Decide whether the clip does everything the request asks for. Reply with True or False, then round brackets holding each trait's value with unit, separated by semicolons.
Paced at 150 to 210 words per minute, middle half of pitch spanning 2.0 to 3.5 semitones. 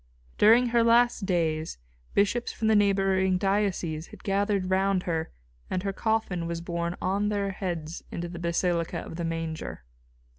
True (155 wpm; 3.1 semitones)